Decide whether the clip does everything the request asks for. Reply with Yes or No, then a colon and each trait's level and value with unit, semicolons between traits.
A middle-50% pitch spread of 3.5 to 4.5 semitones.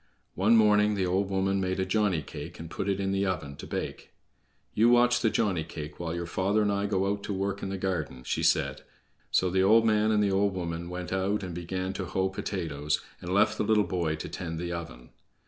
No: average, 2.9 semitones